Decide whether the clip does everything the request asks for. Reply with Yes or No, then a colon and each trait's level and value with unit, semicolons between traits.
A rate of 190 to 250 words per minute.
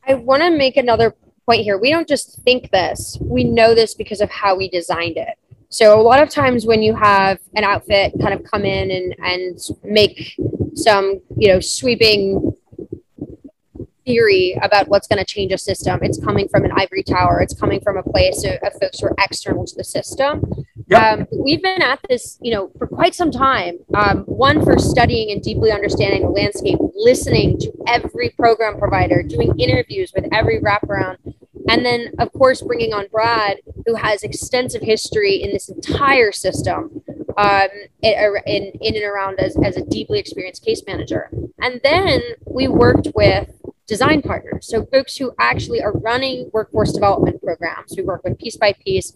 No: average, 180 wpm